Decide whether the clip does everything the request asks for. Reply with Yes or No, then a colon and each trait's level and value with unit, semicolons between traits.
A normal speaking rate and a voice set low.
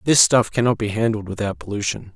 Yes: average, 195 wpm; low, 105 Hz